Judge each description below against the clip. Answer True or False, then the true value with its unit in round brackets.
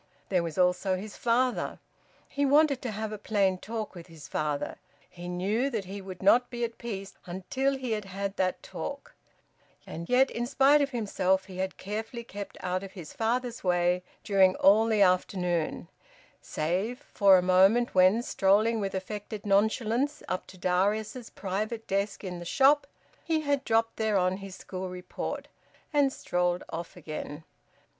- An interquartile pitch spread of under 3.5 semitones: False (4.1 semitones)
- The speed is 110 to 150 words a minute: False (165 wpm)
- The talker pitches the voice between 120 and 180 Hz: False (200 Hz)